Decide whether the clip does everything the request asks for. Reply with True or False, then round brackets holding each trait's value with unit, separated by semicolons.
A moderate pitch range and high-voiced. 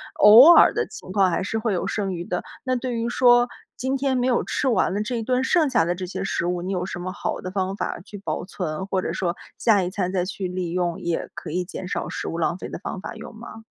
True (4.7 semitones; 195 Hz)